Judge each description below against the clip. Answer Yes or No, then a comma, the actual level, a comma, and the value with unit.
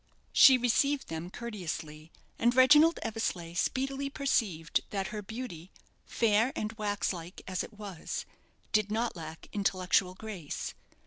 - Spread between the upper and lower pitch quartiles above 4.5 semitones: Yes, average, 5.2 semitones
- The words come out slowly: Yes, slow, 130 wpm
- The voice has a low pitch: No, high, 210 Hz